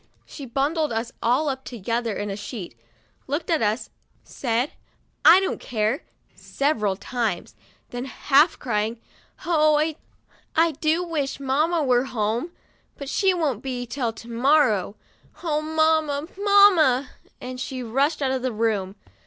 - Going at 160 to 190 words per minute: No, average, 145 wpm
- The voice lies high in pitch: Yes, very high, 270 Hz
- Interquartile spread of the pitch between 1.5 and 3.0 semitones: No, average, 5.0 semitones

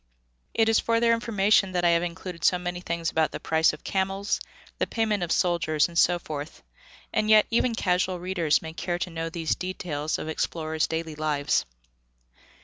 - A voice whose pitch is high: No, medium, 175 Hz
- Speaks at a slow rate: No, average, 185 wpm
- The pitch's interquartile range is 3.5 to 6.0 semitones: No, average, 3.1 semitones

